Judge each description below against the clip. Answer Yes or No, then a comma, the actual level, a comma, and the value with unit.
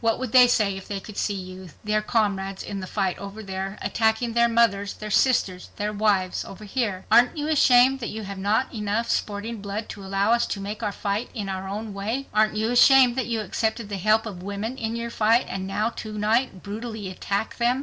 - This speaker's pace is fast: Yes, fast, 220 wpm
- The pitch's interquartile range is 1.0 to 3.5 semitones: Yes, average, 2.8 semitones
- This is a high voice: Yes, high, 215 Hz